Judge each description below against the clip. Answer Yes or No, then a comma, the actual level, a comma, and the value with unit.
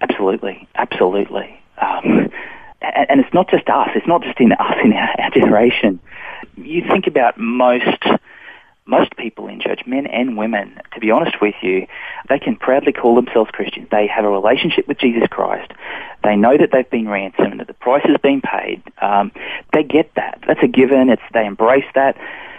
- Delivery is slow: No, average, 180 wpm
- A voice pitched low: Yes, low, 125 Hz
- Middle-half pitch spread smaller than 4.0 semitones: No, wide, 5.4 semitones